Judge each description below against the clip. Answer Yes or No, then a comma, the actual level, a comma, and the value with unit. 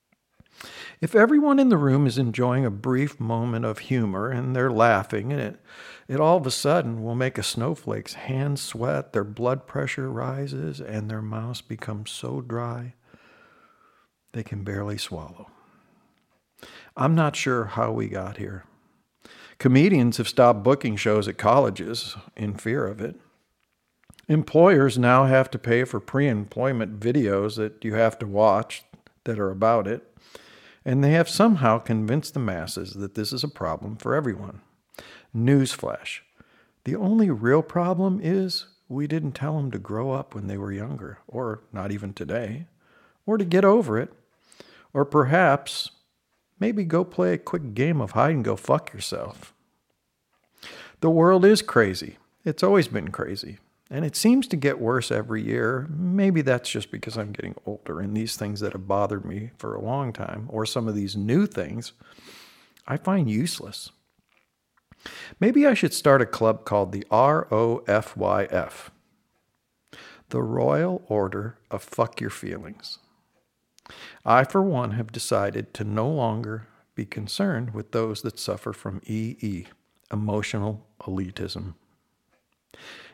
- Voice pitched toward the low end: Yes, low, 115 Hz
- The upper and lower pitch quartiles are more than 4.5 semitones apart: Yes, average, 5.0 semitones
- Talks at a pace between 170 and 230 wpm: No, average, 155 wpm